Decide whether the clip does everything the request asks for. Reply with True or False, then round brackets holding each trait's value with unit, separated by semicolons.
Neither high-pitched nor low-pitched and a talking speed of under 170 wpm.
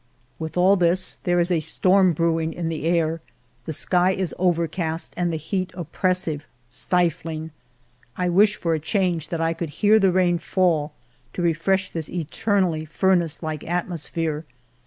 True (170 Hz; 160 wpm)